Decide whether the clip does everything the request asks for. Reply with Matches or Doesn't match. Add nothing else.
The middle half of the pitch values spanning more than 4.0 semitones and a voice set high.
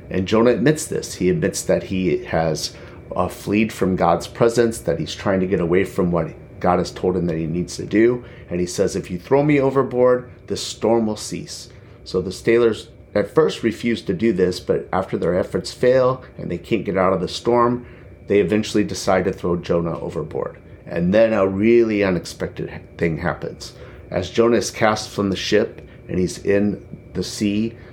Doesn't match